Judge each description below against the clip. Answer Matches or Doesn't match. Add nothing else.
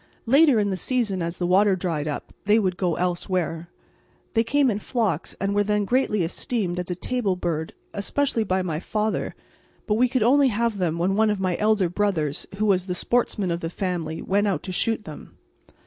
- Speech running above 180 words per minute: Matches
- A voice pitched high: Matches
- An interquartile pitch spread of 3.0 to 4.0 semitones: Matches